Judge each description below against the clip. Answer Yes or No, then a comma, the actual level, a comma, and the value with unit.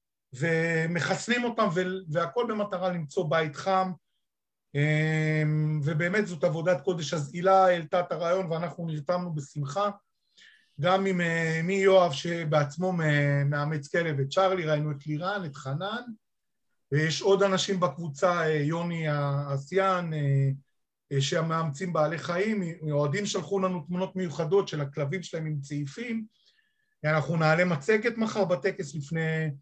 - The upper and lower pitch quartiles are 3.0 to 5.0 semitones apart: Yes, average, 3.9 semitones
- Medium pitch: Yes, medium, 170 Hz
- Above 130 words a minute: No, average, 120 wpm